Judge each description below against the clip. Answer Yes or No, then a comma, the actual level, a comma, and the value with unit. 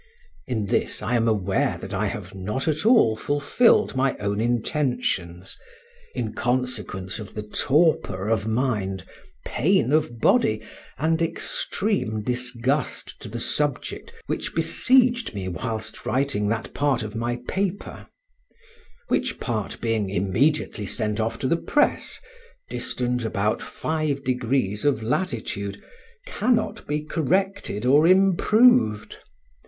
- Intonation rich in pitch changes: Yes, wide, 6.4 semitones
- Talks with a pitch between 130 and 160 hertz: No, low, 120 Hz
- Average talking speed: No, slow, 125 wpm